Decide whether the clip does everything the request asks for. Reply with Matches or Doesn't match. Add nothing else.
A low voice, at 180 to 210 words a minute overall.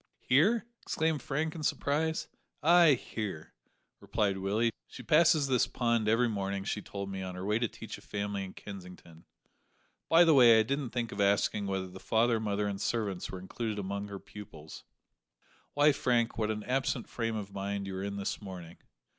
Matches